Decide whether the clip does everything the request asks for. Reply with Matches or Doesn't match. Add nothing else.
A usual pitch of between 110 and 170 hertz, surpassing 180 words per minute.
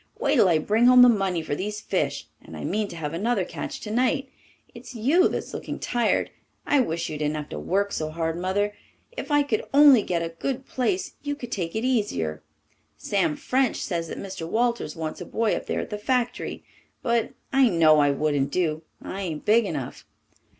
Doesn't match